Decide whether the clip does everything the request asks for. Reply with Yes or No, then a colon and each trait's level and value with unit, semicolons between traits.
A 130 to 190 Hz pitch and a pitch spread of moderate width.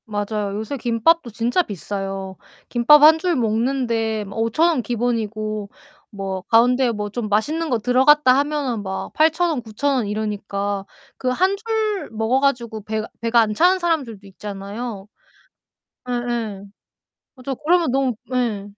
No: high, 235 Hz; average, 4.8 semitones